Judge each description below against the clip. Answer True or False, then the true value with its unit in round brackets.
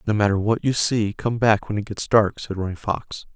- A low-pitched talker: True (105 Hz)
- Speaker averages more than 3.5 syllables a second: True (5.1 syllables/s)